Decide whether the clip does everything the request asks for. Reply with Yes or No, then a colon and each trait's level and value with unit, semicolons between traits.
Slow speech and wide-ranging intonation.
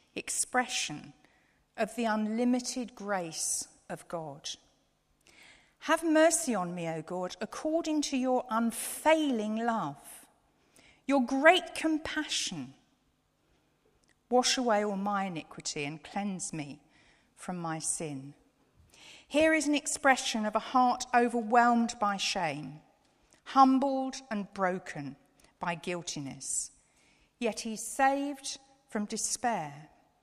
Yes: slow, 105 wpm; wide, 6.5 semitones